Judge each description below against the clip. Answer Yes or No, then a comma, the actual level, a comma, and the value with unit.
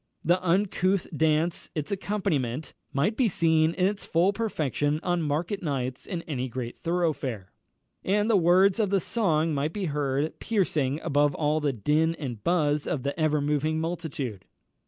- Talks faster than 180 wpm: No, average, 160 wpm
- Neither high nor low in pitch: Yes, medium, 160 Hz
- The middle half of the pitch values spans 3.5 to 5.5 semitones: Yes, average, 4.0 semitones